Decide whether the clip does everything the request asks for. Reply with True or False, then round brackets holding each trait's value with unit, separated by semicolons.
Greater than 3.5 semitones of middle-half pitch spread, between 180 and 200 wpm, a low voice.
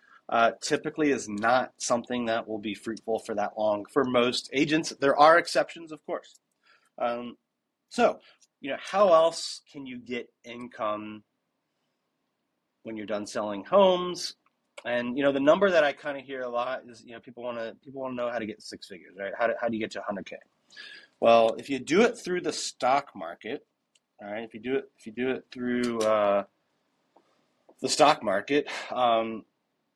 True (3.9 semitones; 190 wpm; 120 Hz)